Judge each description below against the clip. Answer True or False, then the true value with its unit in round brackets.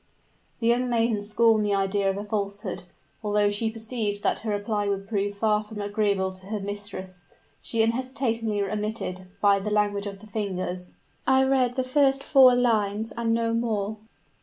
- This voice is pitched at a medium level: False (210 Hz)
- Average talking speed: True (170 wpm)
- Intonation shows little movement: True (2.2 semitones)